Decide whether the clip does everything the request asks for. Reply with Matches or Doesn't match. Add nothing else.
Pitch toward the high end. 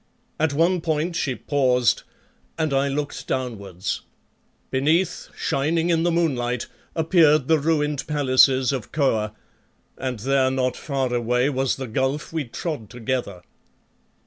Doesn't match